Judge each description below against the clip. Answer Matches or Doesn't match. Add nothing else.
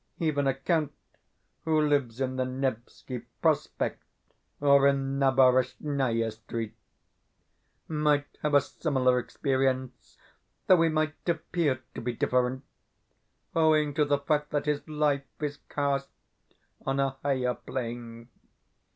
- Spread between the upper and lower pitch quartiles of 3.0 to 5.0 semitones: Doesn't match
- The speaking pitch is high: Doesn't match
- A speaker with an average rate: Doesn't match